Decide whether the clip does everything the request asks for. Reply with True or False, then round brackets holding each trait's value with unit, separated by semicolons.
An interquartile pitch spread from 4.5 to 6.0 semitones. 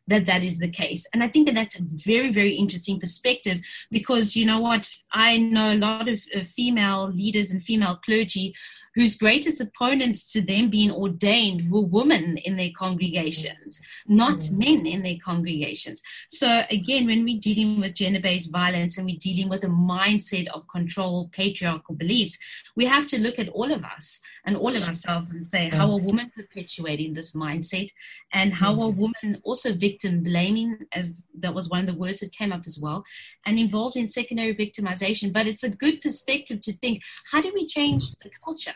False (4.1 semitones)